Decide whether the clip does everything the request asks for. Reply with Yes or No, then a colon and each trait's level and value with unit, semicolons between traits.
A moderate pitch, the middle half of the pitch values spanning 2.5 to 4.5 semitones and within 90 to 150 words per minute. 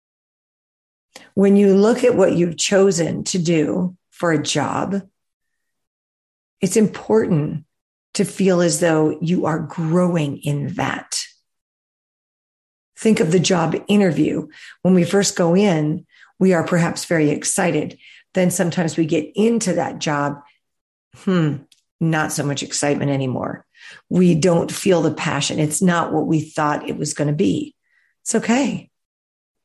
Yes: medium, 170 Hz; average, 4.0 semitones; average, 140 wpm